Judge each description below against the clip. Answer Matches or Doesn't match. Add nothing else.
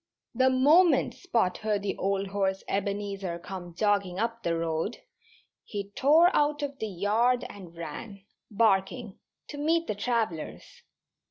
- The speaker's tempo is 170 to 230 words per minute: Doesn't match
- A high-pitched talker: Matches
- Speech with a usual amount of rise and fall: Matches